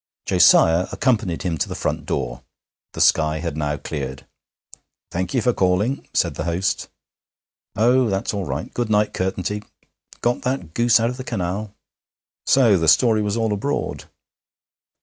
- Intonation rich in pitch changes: Yes, wide, 5.8 semitones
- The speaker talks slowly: No, average, 155 wpm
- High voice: No, low, 100 Hz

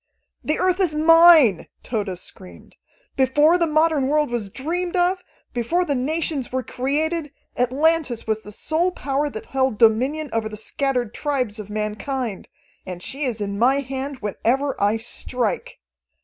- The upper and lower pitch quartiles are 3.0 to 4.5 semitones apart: No, wide, 5.6 semitones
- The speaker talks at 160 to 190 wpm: No, average, 150 wpm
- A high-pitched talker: Yes, very high, 265 Hz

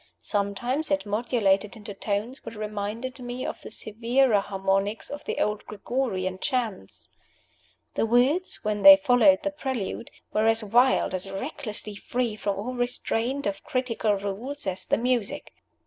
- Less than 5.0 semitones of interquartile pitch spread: Yes, average, 3.9 semitones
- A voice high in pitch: Yes, high, 225 Hz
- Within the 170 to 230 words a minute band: No, average, 145 wpm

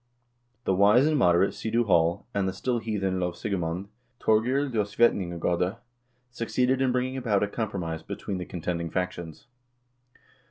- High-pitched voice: No, low, 100 Hz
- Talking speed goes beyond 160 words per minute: No, average, 145 wpm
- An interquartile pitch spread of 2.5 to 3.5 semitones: No, average, 5.0 semitones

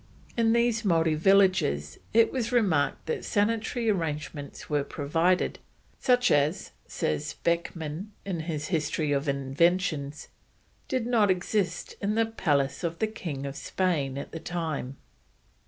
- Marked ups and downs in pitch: Yes, wide, 5.9 semitones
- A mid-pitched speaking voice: Yes, medium, 170 Hz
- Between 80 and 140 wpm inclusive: Yes, slow, 135 wpm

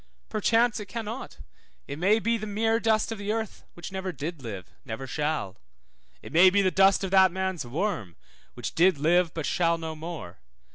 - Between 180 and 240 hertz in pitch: Yes, medium, 185 Hz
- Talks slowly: No, average, 190 wpm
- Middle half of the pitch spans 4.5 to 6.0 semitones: Yes, average, 5.1 semitones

